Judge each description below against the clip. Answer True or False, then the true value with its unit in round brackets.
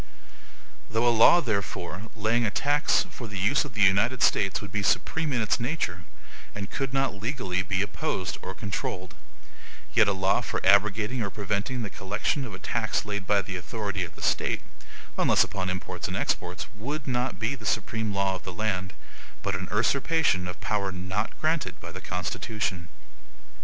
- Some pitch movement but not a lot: True (3.9 semitones)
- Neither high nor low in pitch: False (105 Hz)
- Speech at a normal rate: True (180 wpm)